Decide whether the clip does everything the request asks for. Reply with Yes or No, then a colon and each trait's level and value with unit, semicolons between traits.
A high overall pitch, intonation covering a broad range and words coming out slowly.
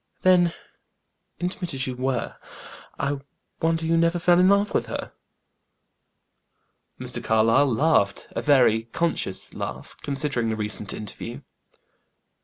No: medium, 140 Hz; wide, 6.7 semitones; slow, 120 wpm